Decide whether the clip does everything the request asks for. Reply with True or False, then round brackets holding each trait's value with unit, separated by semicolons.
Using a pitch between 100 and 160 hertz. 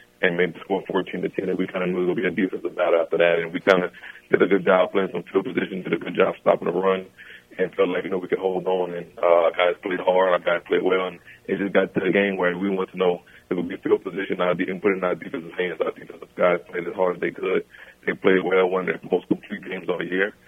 False (90 Hz)